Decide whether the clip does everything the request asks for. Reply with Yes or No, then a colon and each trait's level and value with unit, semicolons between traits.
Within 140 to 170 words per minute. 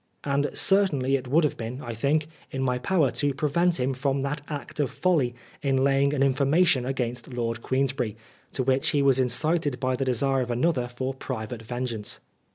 No: average, 185 wpm